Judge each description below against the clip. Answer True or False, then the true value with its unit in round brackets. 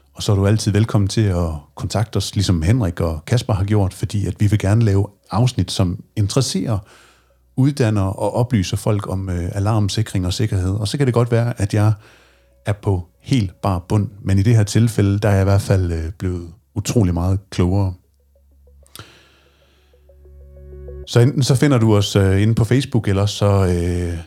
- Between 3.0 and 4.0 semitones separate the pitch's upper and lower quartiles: True (3.6 semitones)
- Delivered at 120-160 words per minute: False (190 wpm)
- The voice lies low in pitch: True (100 Hz)